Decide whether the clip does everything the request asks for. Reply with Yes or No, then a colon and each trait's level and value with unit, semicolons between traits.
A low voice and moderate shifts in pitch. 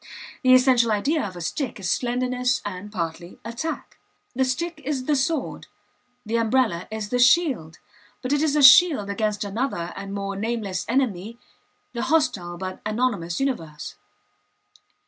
No: high, 235 Hz; average, 5.0 semitones